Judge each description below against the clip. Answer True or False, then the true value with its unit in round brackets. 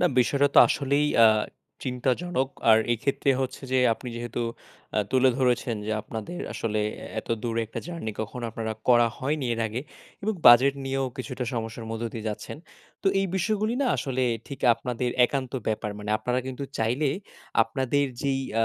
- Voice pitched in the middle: False (125 Hz)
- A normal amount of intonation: True (3.3 semitones)